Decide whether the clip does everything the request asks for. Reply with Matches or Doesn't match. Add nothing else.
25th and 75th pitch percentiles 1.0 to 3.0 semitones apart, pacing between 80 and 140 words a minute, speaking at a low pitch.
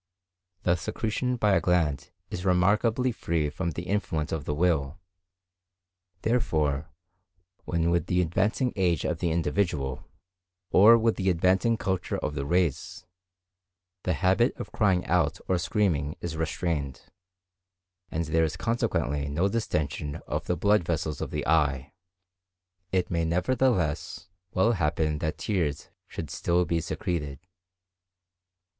Doesn't match